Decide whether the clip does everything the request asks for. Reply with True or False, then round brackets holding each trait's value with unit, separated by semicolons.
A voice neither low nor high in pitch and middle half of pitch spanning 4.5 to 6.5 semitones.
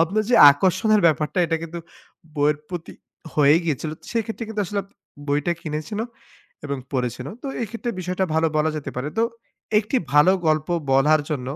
True (160 Hz; 4.8 semitones)